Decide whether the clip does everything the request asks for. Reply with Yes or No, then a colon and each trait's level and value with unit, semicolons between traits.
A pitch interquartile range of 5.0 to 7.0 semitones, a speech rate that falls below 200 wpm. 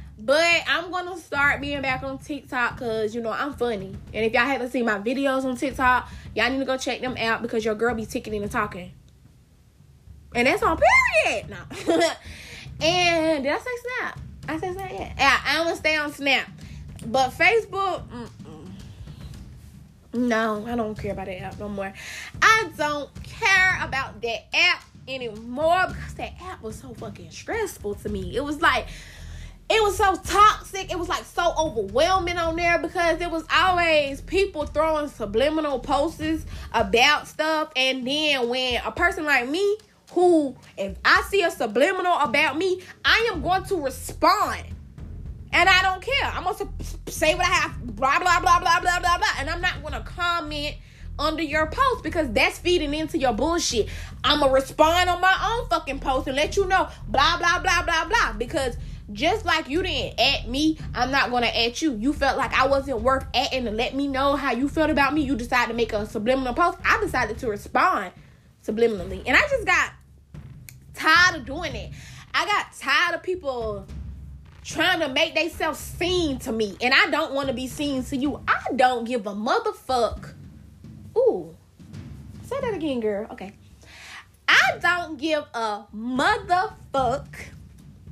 Yes: wide, 5.6 semitones; average, 180 wpm